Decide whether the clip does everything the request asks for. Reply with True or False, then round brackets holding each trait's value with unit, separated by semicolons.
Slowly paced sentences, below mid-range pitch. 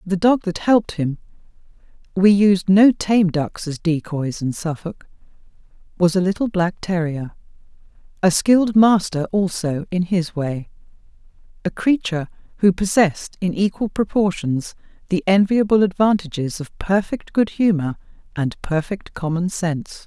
False (130 wpm; 185 Hz)